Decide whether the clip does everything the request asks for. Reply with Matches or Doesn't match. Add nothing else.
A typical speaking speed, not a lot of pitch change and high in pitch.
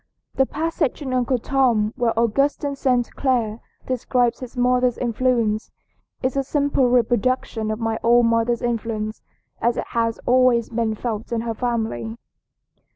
Matches